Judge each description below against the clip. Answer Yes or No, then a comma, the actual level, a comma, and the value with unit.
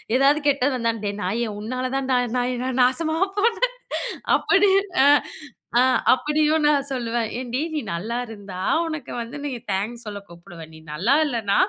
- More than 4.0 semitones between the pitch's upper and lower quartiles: Yes, average, 4.4 semitones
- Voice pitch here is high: Yes, very high, 250 Hz